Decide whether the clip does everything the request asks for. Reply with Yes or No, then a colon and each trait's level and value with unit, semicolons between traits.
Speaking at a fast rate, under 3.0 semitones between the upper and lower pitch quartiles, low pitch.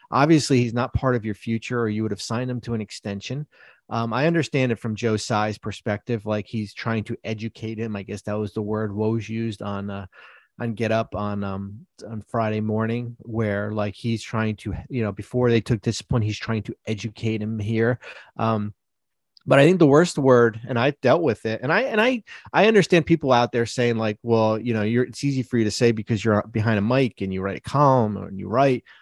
Yes: fast, 230 wpm; narrow, 2.5 semitones; low, 115 Hz